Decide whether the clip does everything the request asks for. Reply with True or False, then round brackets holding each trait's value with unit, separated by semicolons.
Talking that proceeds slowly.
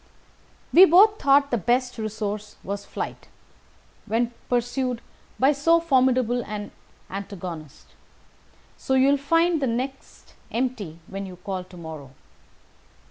True (125 wpm)